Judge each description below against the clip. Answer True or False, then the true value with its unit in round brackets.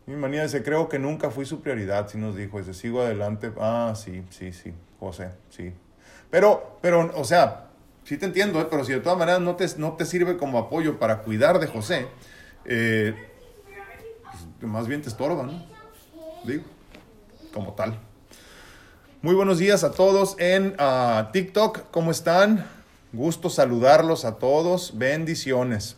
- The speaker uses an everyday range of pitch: False (8.3 semitones)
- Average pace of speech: True (160 wpm)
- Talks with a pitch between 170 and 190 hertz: False (145 Hz)